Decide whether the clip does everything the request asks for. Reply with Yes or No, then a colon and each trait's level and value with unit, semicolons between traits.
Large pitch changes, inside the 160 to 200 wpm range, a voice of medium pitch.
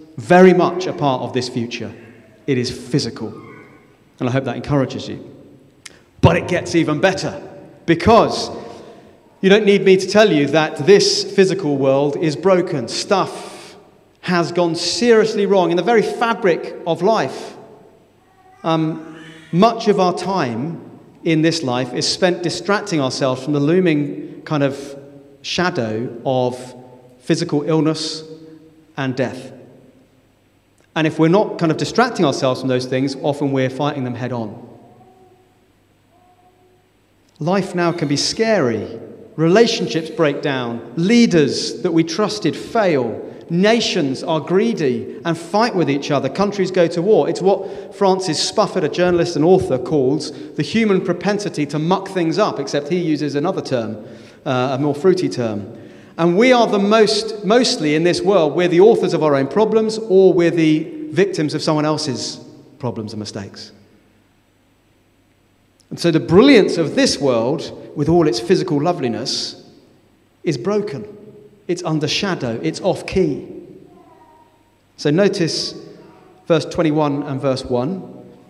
No: wide, 6.1 semitones; average, 145 wpm; medium, 155 Hz